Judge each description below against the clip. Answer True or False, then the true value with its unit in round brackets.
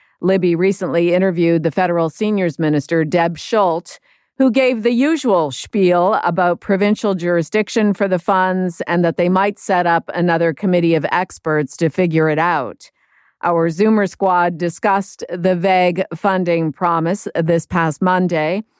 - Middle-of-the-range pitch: True (180 Hz)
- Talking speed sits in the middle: True (145 wpm)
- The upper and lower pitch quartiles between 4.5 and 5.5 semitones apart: False (2.6 semitones)